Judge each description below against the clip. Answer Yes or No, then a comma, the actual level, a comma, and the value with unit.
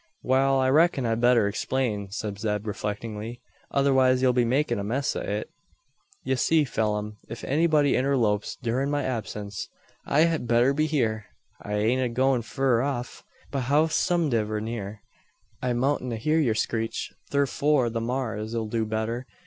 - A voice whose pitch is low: Yes, low, 120 Hz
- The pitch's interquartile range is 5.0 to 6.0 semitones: No, average, 3.8 semitones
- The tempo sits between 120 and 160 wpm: Yes, average, 155 wpm